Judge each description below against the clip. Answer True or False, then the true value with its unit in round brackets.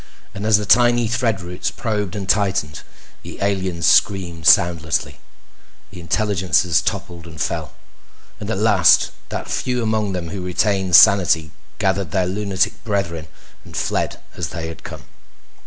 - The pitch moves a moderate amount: True (3.2 semitones)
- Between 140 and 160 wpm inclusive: True (145 wpm)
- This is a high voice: False (95 Hz)